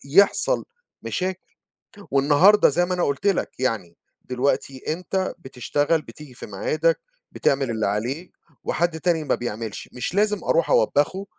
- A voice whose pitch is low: No, medium, 155 Hz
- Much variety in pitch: Yes, wide, 6.1 semitones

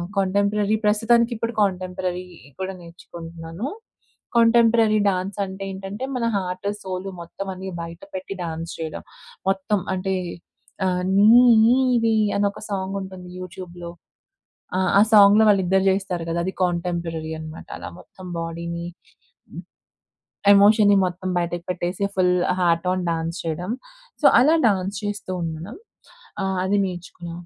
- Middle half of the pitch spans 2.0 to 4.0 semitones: Yes, average, 2.7 semitones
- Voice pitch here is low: No, high, 190 Hz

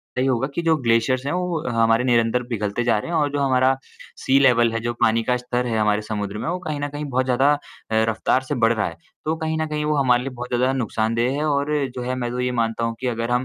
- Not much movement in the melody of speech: No, average, 3.3 semitones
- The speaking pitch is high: No, low, 125 Hz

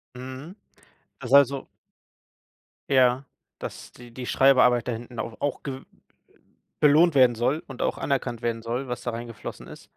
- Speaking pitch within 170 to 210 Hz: No, low, 125 Hz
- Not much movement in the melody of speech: Yes, narrow, 2.3 semitones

